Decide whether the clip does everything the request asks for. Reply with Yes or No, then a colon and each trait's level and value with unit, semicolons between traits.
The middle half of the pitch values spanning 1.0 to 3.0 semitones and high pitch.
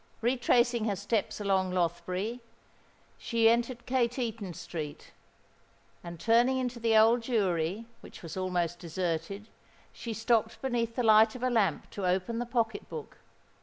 No: average, 4.3 semitones; high, 225 Hz